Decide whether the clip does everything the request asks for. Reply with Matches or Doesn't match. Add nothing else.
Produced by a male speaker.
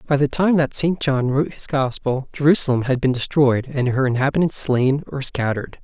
Matches